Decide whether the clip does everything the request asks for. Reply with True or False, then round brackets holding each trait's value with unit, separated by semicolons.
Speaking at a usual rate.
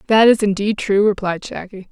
True (190 wpm)